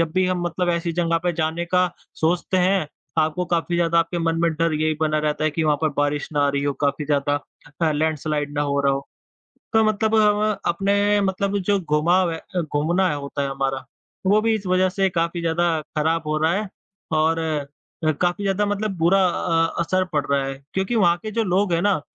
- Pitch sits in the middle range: Yes, medium, 170 Hz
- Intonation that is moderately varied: Yes, average, 3.3 semitones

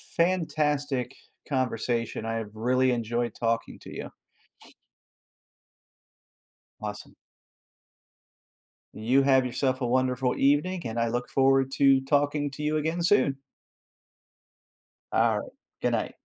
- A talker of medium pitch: No, low, 130 Hz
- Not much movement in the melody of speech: No, average, 3.2 semitones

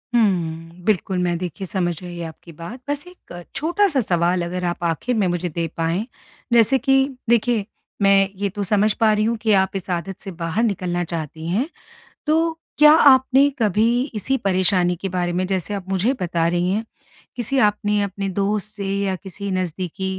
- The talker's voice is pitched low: No, high, 195 Hz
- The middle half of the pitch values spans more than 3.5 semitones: Yes, average, 4.0 semitones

